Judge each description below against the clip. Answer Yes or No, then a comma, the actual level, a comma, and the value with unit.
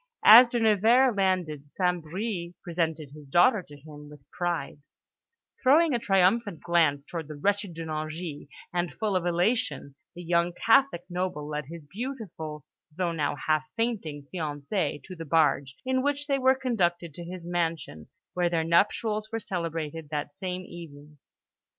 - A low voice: No, medium, 175 Hz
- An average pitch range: Yes, average, 5.0 semitones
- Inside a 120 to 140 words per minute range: No, average, 155 wpm